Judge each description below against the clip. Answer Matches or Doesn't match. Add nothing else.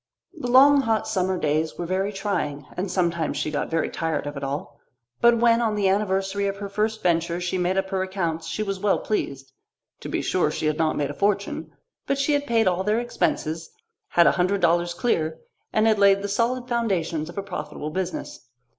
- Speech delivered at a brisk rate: Matches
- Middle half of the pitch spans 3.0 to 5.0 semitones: Matches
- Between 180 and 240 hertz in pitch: Matches